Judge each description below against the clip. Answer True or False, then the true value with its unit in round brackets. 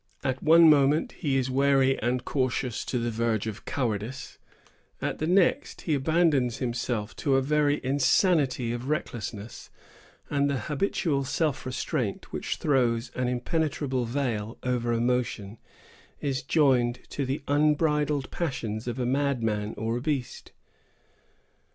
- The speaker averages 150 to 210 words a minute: False (135 wpm)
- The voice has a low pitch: True (130 Hz)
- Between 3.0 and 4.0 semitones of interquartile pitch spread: True (3.3 semitones)